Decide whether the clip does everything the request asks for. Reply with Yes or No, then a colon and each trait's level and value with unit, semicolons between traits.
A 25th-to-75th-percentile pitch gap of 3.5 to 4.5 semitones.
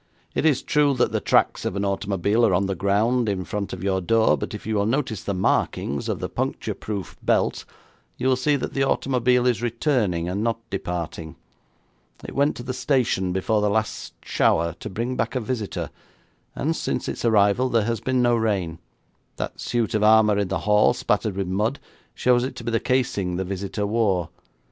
Yes: average, 4.0 semitones